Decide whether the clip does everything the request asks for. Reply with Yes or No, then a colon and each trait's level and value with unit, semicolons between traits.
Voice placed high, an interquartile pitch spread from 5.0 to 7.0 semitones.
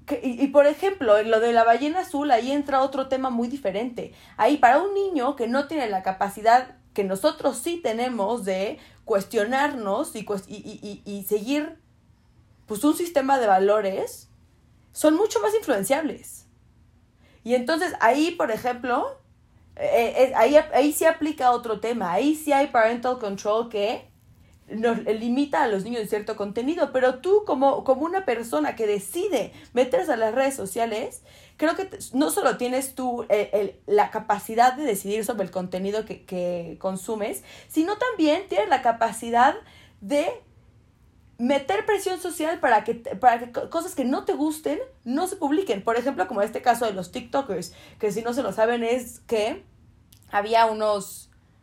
Yes: high, 245 Hz; wide, 5.5 semitones